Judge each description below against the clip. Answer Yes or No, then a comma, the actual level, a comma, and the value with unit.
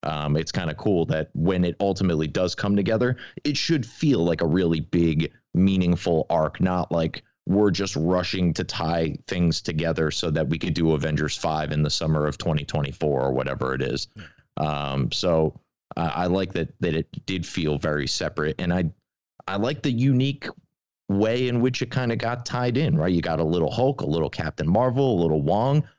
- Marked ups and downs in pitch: Yes, wide, 6.3 semitones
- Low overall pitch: Yes, very low, 90 Hz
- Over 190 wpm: Yes, fast, 205 wpm